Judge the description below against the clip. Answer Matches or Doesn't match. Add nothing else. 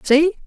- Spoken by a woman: Matches